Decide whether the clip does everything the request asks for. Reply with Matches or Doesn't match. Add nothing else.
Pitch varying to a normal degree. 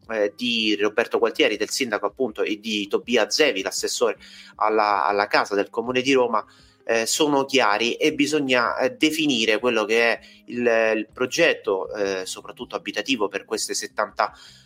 Matches